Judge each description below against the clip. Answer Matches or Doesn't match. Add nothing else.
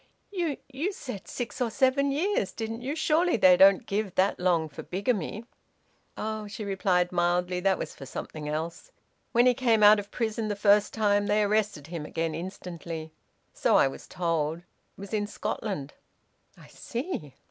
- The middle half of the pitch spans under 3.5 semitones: Doesn't match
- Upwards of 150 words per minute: Matches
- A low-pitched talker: Doesn't match